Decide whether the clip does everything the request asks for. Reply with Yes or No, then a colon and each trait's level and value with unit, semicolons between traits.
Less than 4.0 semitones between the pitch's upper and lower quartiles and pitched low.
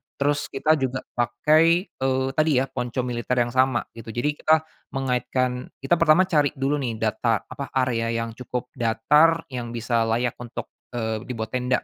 Yes: average, 3.3 semitones; low, 125 Hz